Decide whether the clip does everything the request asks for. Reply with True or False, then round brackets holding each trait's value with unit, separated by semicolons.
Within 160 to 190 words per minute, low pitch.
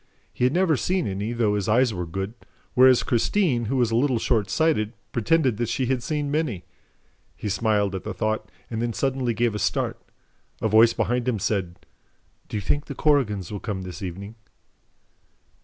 True (185 wpm; 115 Hz)